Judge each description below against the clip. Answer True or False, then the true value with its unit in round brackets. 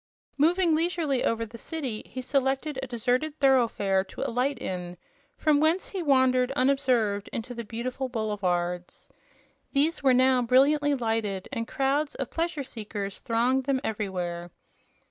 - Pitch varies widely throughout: False (4.2 semitones)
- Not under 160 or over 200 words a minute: False (140 wpm)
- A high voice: True (255 Hz)